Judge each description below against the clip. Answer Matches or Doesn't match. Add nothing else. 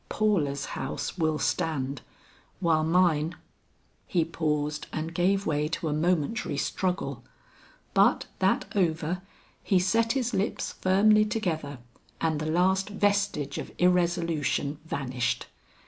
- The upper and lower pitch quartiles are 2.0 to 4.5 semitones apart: Matches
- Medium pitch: Matches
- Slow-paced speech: Matches